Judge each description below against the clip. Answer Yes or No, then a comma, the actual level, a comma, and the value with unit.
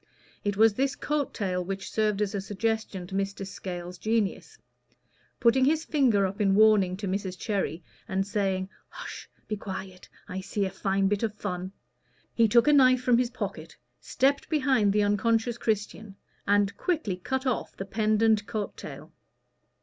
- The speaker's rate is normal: Yes, average, 165 wpm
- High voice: Yes, high, 205 Hz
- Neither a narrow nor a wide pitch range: Yes, average, 3.1 semitones